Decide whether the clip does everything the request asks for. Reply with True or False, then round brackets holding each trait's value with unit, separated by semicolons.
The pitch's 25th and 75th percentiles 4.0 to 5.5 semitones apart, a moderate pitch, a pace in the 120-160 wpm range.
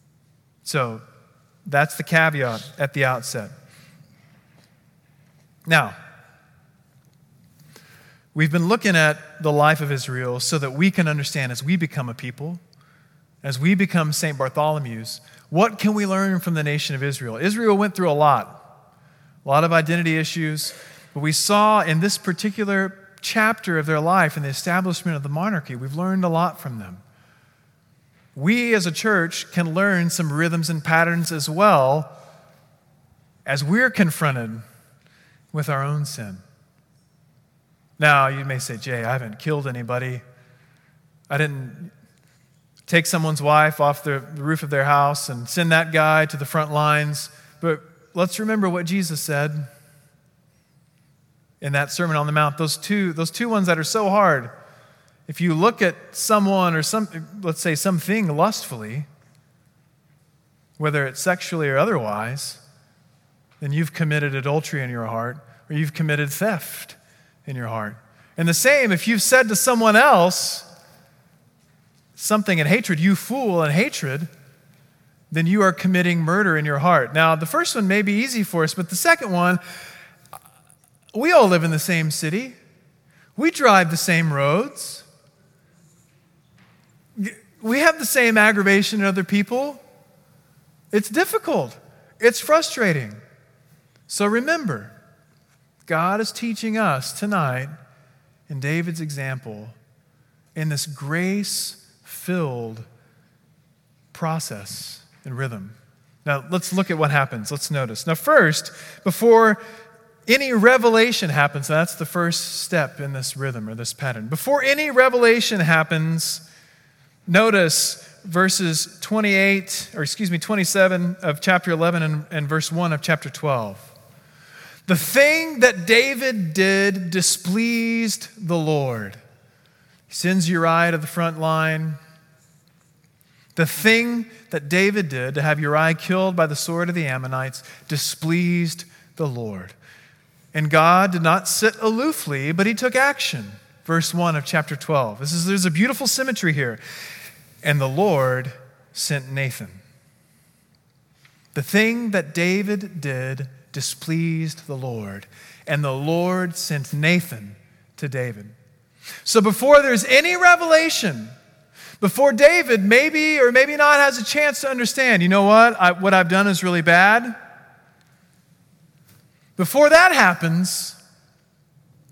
True (4.4 semitones; 160 Hz; 140 wpm)